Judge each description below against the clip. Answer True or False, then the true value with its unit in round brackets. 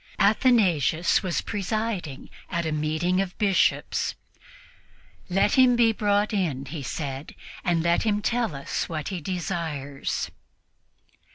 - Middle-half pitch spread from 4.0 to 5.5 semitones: True (5.1 semitones)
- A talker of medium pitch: True (180 Hz)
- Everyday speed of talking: False (120 wpm)